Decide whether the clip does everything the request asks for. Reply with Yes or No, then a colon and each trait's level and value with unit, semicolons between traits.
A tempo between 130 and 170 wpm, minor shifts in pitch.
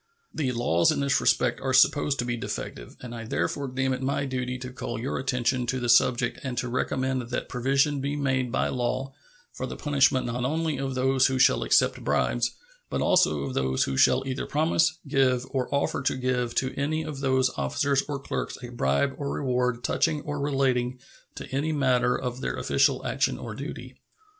No: average, 195 wpm; narrow, 2.0 semitones